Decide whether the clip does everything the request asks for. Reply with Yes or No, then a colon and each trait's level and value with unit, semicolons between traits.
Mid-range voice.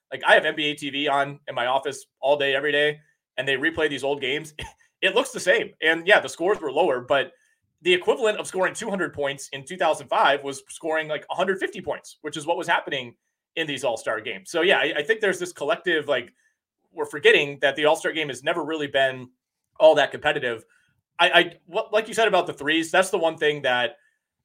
Yes: medium, 160 Hz